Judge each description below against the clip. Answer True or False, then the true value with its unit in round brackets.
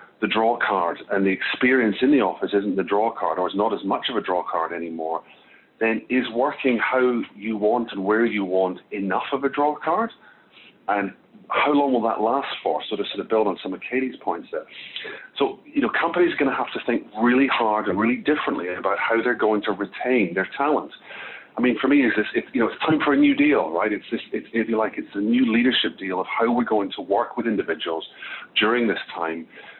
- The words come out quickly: True (230 wpm)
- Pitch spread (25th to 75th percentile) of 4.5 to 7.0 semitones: True (5.4 semitones)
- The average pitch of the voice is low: True (115 Hz)